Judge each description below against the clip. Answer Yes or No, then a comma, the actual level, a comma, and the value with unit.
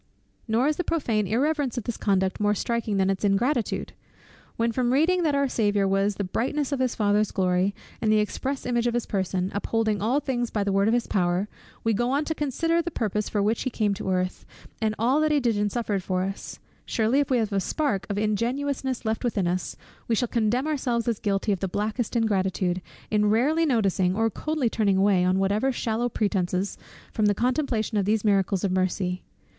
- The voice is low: No, high, 220 Hz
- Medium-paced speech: No, fast, 210 wpm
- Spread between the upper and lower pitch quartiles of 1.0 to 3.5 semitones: No, average, 4.0 semitones